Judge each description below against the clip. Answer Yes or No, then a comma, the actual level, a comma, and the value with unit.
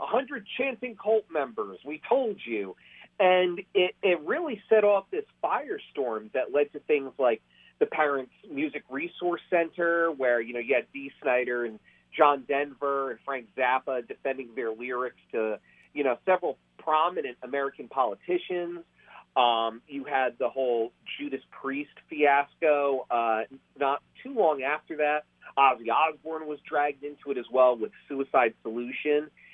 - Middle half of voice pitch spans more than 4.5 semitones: Yes, average, 5.2 semitones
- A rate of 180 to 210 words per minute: No, average, 150 wpm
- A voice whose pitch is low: No, medium, 145 Hz